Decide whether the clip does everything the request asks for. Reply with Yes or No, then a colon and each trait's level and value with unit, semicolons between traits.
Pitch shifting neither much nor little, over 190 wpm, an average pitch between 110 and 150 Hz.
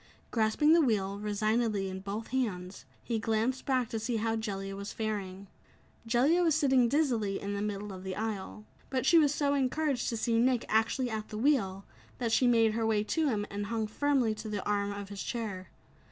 No: average, 3.8 semitones; average, 200 wpm; high, 220 Hz